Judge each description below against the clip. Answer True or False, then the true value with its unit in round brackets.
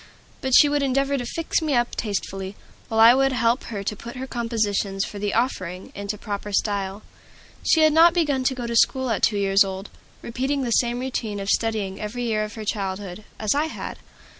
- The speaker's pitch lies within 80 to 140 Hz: False (225 Hz)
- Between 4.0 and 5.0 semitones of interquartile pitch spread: True (4.5 semitones)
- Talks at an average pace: False (210 wpm)